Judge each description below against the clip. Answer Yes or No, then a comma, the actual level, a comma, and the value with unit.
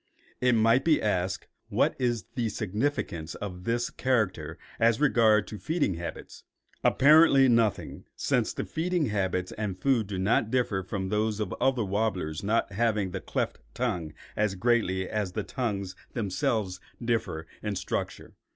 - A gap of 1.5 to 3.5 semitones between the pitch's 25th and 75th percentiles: No, average, 4.2 semitones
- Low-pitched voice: Yes, low, 105 Hz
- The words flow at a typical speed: Yes, average, 145 wpm